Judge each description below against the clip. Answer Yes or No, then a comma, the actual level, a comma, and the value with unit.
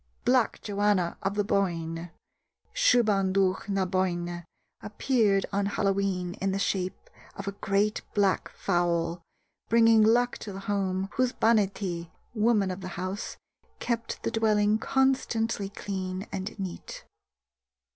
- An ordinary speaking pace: No, slow, 125 wpm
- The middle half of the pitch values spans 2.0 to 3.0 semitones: Yes, narrow, 2.6 semitones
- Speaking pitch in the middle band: No, high, 200 Hz